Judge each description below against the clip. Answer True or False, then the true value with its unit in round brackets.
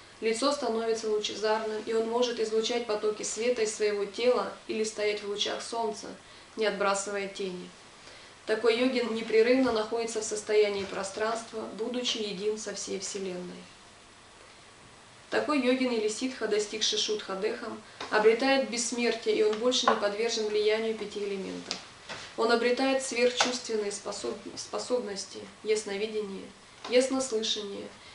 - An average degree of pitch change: False (2.2 semitones)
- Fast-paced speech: False (115 wpm)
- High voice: True (220 Hz)